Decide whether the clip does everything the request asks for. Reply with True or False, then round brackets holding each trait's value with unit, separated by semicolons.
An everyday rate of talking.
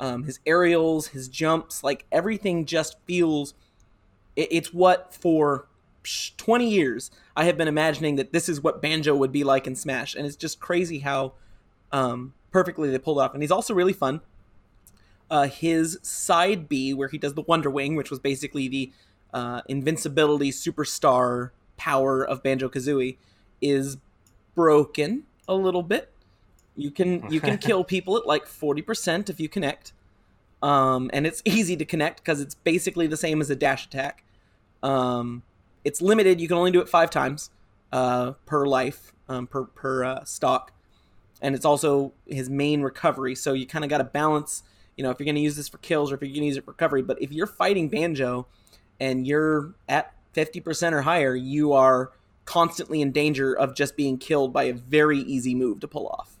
True (185 wpm)